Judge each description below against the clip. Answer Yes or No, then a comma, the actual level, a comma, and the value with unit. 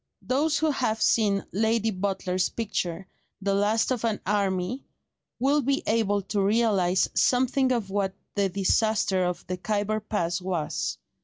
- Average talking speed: Yes, average, 145 wpm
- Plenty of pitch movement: No, average, 3.3 semitones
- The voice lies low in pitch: No, high, 205 Hz